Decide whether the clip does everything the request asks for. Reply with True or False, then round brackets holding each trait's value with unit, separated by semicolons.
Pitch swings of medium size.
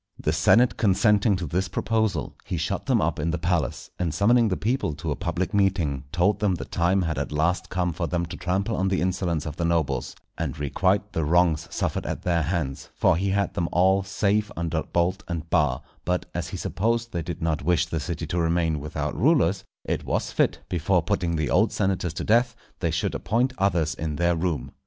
True (3.2 semitones)